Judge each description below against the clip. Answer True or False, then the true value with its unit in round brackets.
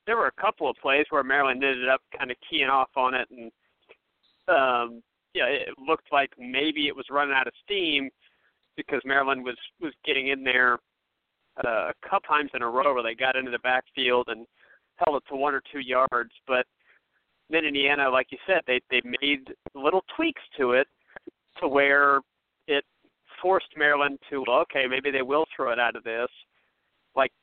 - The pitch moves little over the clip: True (2.3 semitones)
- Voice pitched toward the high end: False (135 Hz)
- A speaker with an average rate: True (190 wpm)